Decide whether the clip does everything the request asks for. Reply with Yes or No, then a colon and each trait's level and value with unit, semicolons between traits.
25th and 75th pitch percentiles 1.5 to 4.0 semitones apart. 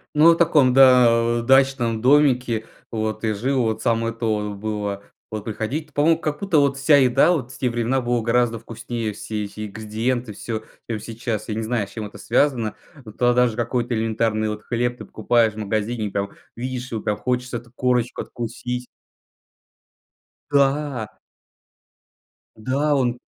Yes: average, 2.8 semitones